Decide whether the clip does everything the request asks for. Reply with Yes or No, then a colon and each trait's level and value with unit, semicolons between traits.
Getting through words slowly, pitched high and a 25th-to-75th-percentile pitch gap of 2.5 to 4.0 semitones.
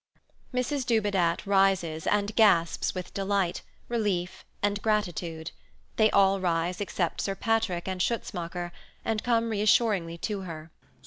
Yes: slow, 125 wpm; high, 195 Hz; average, 3.6 semitones